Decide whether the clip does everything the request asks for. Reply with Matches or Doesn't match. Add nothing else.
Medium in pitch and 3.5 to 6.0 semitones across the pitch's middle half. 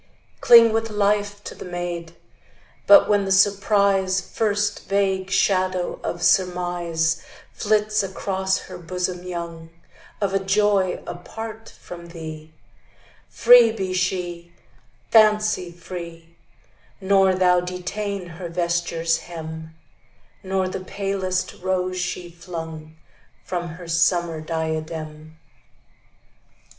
Doesn't match